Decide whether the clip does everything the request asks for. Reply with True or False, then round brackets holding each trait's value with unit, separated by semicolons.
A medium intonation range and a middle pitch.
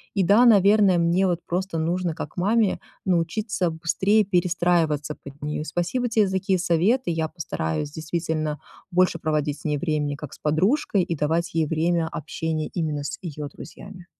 True (3.3 semitones; 170 Hz)